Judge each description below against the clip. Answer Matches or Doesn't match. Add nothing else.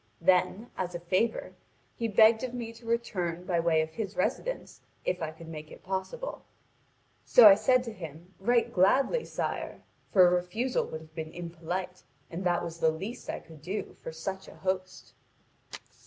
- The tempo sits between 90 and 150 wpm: Doesn't match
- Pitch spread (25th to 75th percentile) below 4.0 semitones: Doesn't match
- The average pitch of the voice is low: Doesn't match